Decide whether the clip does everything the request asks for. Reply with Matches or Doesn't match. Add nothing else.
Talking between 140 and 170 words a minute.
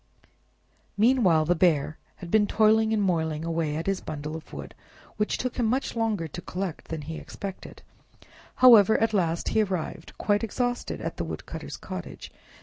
Matches